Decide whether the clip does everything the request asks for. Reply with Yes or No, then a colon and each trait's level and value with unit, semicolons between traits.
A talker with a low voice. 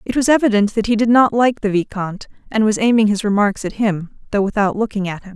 No: high, 210 Hz